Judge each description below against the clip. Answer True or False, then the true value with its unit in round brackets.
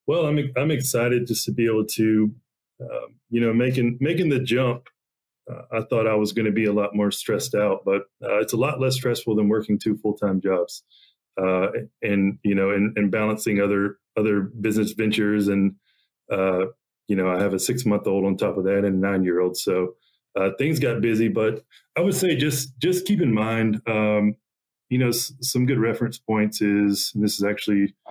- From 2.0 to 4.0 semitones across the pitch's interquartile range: True (3.0 semitones)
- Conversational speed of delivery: False (210 wpm)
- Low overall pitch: True (110 Hz)